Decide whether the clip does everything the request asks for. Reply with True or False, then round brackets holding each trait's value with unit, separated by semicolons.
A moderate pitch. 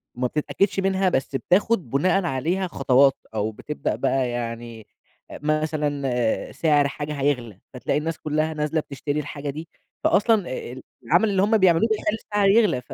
True (150 Hz)